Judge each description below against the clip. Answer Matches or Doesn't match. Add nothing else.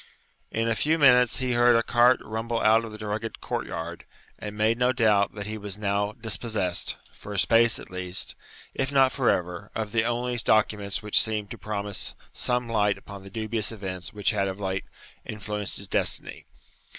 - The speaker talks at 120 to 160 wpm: Doesn't match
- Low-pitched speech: Matches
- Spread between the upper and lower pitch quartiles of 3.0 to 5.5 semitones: Doesn't match